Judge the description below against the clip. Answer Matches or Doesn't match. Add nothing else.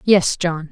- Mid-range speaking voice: Matches